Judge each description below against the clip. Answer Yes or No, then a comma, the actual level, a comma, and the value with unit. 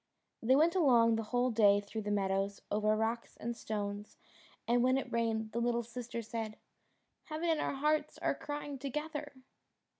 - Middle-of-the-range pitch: No, high, 235 Hz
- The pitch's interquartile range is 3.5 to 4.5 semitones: Yes, average, 4.0 semitones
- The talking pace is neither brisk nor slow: Yes, average, 160 wpm